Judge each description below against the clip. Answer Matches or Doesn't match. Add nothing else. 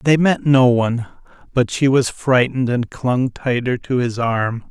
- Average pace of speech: Matches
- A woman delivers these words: Doesn't match